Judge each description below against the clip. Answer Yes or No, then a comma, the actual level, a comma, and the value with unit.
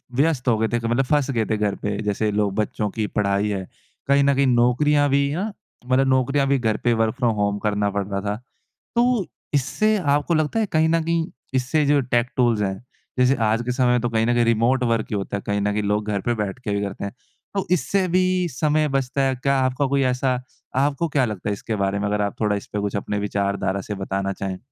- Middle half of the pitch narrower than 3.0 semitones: No, average, 5.2 semitones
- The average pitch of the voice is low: Yes, low, 120 Hz